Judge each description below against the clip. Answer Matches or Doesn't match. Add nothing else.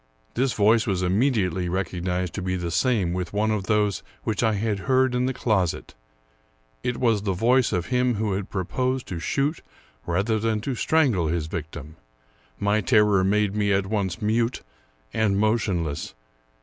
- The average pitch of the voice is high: Doesn't match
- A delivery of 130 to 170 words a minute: Matches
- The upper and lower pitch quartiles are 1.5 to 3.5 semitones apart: Doesn't match